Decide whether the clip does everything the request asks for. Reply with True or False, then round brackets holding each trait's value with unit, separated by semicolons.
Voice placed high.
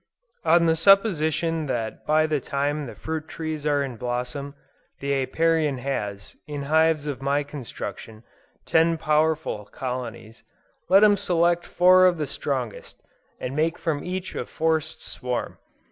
False (150 Hz)